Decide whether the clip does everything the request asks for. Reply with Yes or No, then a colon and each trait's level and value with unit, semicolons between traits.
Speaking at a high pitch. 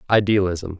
No: very low, 95 Hz